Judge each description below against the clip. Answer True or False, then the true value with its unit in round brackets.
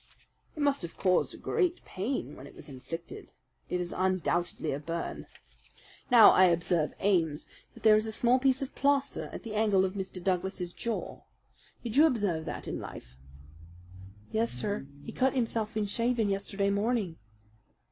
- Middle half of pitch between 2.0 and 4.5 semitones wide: False (5.3 semitones)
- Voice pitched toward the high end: True (200 Hz)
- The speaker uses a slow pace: False (165 wpm)